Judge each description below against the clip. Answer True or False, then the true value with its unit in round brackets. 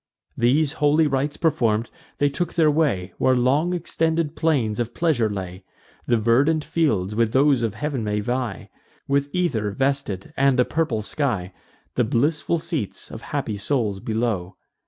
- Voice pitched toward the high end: False (130 Hz)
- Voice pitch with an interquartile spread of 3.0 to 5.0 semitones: False (5.6 semitones)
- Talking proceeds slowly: False (155 wpm)